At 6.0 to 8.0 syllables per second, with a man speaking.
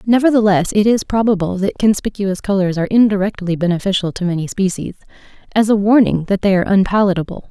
No: 6.5 syllables/s; female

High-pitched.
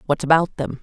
No: medium, 155 Hz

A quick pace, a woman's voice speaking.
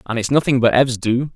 No: fast, 265 wpm; male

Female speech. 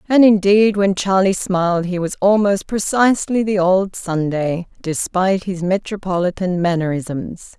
Yes: female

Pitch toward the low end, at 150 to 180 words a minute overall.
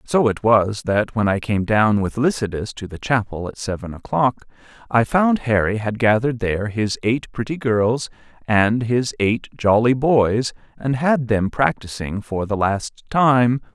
Yes: low, 115 Hz; average, 170 wpm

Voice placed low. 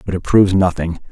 Yes: very low, 90 Hz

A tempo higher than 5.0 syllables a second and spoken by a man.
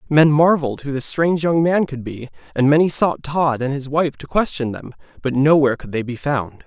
Yes: 5.4 syllables/s; male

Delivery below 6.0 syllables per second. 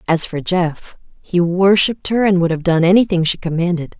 Yes: 5.3 syllables/s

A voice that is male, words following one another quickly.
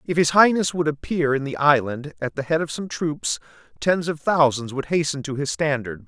Yes: male; fast, 215 wpm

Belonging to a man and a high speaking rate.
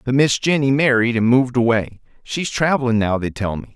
No: male; average, 190 wpm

